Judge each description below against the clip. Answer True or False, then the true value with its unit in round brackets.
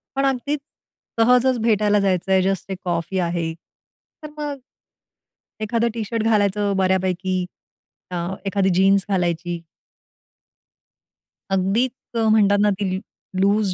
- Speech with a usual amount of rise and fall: True (3.0 semitones)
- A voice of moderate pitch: False (195 Hz)